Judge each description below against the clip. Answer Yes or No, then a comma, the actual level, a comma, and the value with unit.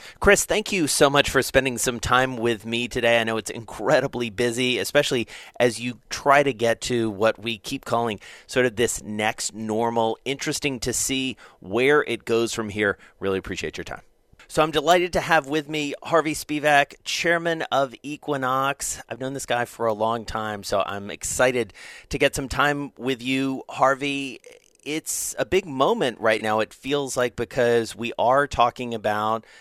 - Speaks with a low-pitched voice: Yes, low, 125 Hz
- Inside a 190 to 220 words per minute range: No, average, 180 wpm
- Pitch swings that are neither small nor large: Yes, average, 3.8 semitones